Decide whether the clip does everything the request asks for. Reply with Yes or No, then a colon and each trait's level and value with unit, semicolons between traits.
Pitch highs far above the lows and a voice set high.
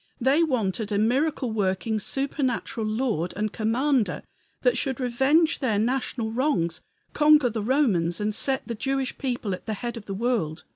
No: average, 4.2 semitones; high, 235 Hz